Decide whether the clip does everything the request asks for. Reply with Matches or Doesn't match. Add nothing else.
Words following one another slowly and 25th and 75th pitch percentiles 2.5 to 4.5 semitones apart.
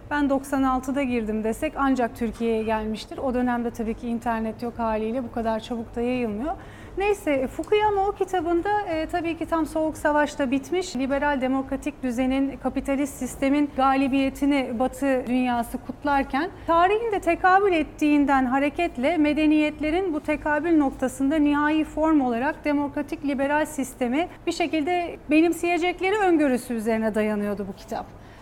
Doesn't match